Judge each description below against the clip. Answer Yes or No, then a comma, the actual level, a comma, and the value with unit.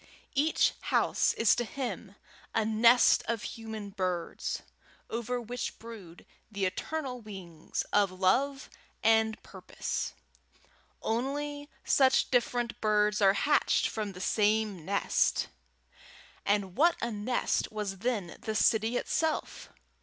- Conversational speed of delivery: No, slow, 115 wpm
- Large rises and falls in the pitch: No, average, 3.5 semitones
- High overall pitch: Yes, high, 220 Hz